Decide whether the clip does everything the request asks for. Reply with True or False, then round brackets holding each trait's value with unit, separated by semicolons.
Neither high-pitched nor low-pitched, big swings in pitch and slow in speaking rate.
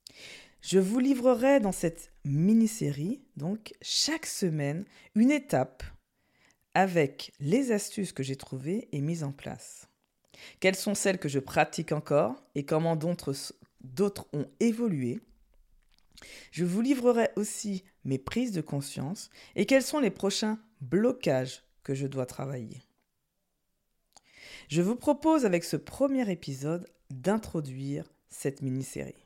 True (175 Hz; 7.3 semitones; 125 wpm)